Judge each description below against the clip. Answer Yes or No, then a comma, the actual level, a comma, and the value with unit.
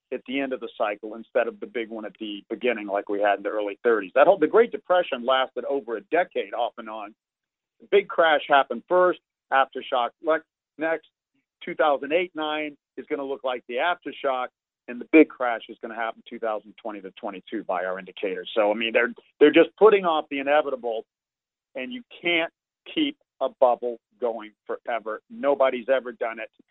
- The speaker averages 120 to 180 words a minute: No, fast, 205 wpm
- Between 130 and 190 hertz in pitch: Yes, low, 135 Hz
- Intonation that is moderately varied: No, wide, 6.1 semitones